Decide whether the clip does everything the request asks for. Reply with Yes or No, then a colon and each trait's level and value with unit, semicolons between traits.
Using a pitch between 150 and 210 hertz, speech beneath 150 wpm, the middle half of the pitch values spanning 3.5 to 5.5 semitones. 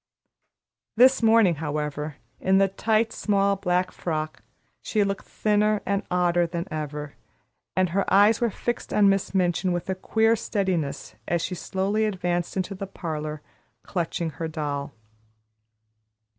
Yes: medium, 185 Hz; average, 140 wpm; average, 3.8 semitones